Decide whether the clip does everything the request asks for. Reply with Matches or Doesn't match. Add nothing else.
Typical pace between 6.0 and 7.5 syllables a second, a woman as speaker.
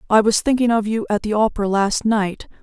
Doesn't match